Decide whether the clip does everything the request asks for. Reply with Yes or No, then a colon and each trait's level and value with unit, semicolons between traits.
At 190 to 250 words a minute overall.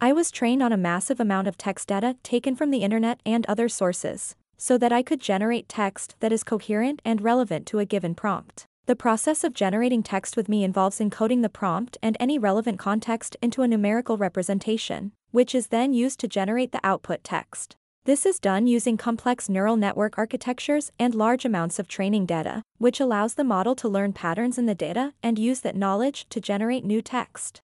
Yes: average, 200 wpm